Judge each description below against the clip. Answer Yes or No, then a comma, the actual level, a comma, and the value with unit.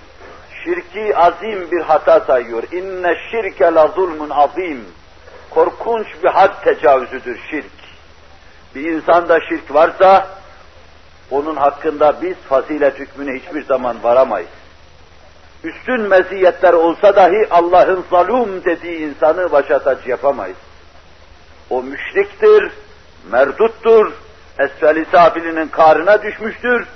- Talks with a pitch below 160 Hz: No, medium, 165 Hz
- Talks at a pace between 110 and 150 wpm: No, average, 100 wpm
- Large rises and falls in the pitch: Yes, wide, 6.6 semitones